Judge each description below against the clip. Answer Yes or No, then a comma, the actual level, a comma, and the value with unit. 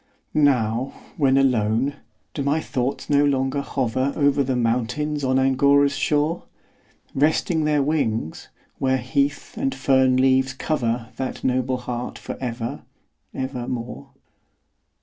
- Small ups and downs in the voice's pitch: Yes, narrow, 2.2 semitones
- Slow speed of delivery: Yes, slow, 125 wpm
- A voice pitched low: Yes, low, 130 Hz